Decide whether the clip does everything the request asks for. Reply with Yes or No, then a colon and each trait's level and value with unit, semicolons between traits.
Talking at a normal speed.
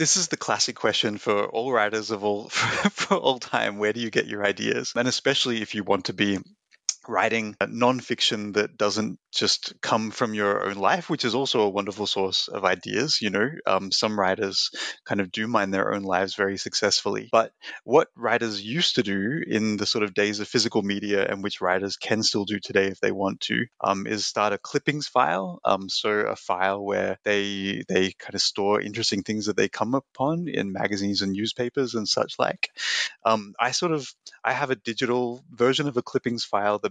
No: fast, 210 wpm